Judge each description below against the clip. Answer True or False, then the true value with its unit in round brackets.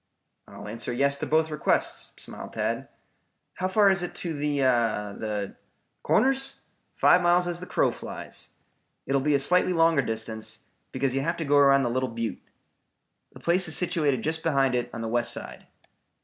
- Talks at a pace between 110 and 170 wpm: False (185 wpm)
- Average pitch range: False (5.9 semitones)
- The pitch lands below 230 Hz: True (140 Hz)